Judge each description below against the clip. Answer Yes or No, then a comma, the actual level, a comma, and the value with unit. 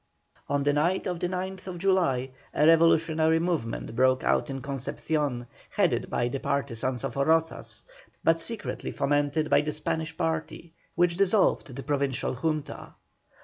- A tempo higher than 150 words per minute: No, average, 145 wpm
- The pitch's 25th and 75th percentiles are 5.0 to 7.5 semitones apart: No, average, 3.4 semitones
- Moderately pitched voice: Yes, medium, 155 Hz